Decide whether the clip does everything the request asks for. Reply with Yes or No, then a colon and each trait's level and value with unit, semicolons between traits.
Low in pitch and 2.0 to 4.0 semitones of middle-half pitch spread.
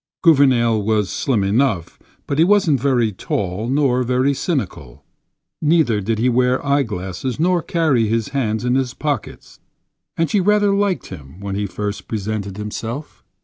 No: low, 125 Hz; average, 5.3 semitones